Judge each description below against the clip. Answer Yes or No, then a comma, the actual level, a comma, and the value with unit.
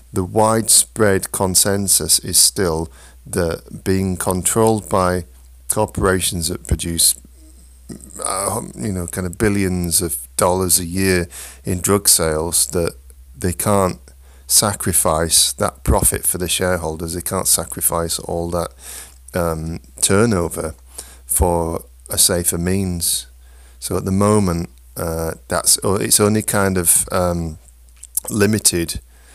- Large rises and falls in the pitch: Yes, wide, 6.0 semitones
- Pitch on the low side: Yes, very low, 85 Hz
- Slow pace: Yes, slow, 115 wpm